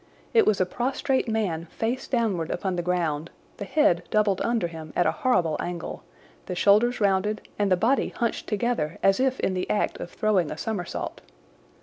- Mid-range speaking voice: No, high, 200 Hz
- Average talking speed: Yes, average, 185 wpm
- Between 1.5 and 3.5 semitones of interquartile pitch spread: No, average, 4.8 semitones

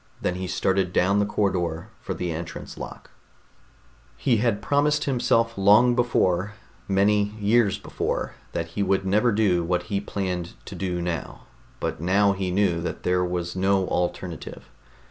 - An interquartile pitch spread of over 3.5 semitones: No, average, 2.8 semitones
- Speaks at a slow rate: No, average, 155 wpm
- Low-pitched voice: Yes, very low, 95 Hz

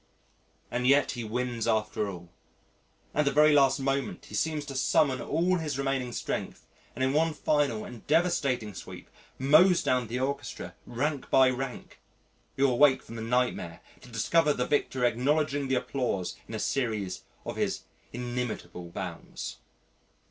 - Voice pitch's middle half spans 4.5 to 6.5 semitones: No, average, 3.3 semitones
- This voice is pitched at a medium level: No, low, 130 Hz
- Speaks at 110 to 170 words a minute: Yes, average, 155 wpm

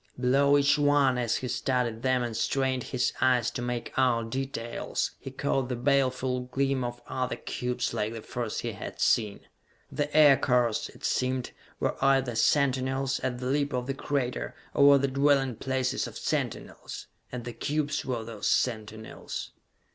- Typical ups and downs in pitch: No, narrow, 2.0 semitones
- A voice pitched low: Yes, low, 130 Hz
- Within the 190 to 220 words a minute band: No, average, 165 wpm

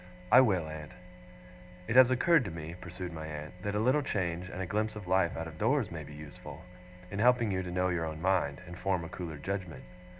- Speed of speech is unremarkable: No, fast, 230 wpm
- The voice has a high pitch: No, very low, 90 Hz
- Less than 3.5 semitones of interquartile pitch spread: No, average, 4.1 semitones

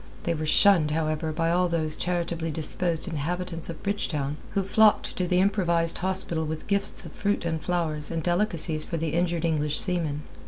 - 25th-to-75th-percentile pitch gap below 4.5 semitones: Yes, narrow, 2.5 semitones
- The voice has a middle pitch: Yes, medium, 170 Hz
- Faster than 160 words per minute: Yes, average, 180 wpm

